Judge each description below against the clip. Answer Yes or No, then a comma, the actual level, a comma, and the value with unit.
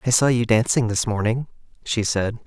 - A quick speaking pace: No, average, 195 wpm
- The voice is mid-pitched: No, low, 115 Hz